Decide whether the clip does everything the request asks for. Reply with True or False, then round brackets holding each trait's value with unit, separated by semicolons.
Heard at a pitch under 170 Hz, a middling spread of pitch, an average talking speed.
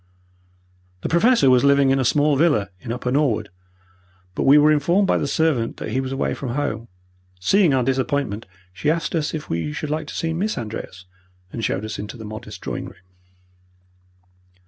True (140 Hz; 4.7 semitones; 190 wpm)